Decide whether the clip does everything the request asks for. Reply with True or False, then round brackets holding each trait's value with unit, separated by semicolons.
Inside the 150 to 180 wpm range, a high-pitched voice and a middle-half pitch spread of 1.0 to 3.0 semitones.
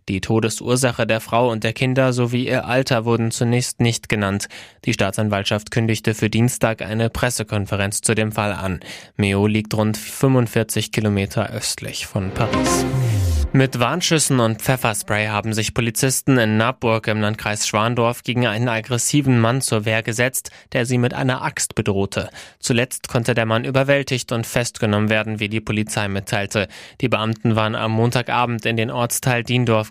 False (160 wpm; 115 Hz; 2.4 semitones)